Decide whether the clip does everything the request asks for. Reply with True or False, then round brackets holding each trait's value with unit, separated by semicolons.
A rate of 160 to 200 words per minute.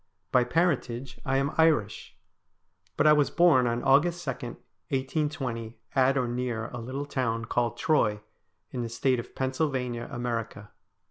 False (145 wpm)